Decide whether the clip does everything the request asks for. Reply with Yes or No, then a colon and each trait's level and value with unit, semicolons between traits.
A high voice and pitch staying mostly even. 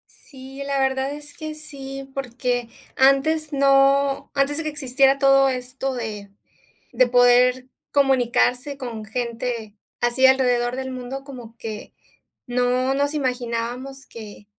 Yes: very high, 265 Hz; narrow, 2.0 semitones